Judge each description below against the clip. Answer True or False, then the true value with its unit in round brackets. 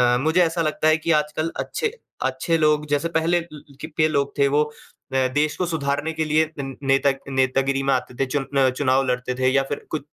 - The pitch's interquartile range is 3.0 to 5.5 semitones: False (2.6 semitones)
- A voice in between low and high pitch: True (150 Hz)